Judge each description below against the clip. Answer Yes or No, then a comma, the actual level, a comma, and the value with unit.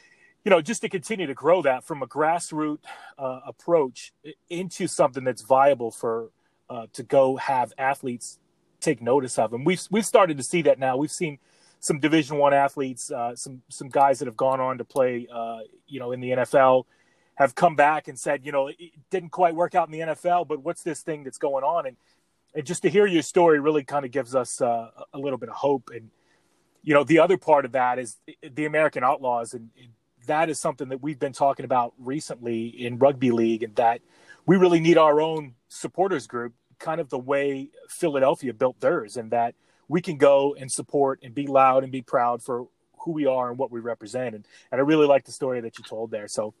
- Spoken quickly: Yes, fast, 220 wpm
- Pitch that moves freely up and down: No, average, 4.0 semitones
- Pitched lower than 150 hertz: Yes, medium, 140 Hz